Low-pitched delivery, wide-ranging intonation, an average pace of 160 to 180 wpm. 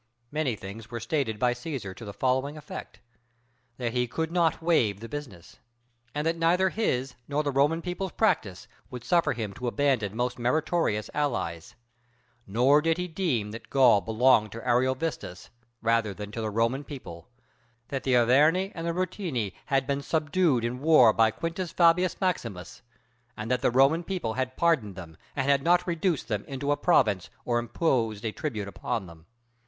Yes: low, 130 Hz; wide, 6.2 semitones; average, 175 wpm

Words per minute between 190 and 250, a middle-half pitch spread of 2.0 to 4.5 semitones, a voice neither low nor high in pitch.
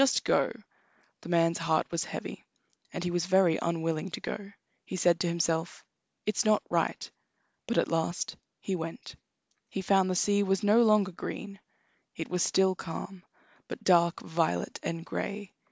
No: average, 165 wpm; average, 2.9 semitones; medium, 180 Hz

